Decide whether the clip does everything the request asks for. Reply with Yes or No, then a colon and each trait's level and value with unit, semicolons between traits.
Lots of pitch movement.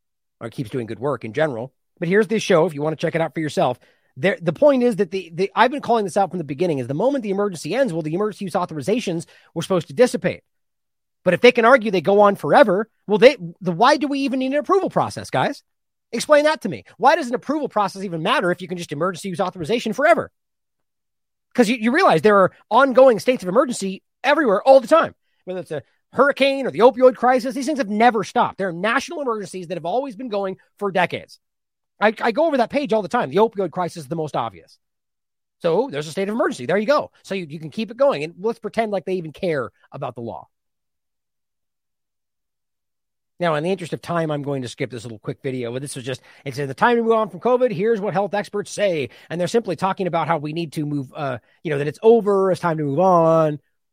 Yes: wide, 6.3 semitones